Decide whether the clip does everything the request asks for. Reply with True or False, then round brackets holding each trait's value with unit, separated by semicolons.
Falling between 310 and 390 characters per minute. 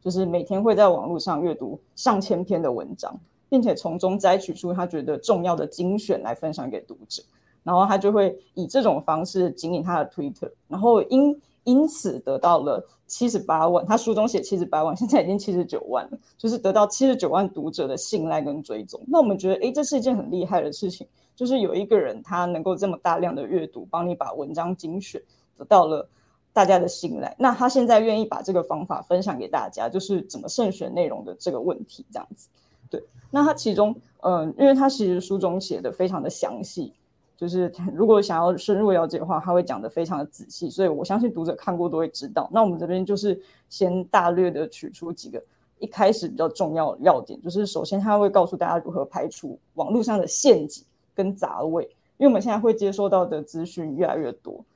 True (325 characters per minute)